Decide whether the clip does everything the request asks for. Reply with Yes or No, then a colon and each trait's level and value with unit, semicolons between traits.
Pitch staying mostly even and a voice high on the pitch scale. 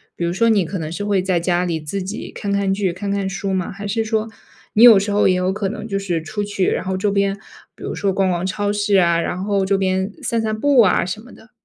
Yes: narrow, 1.9 semitones; high, 195 Hz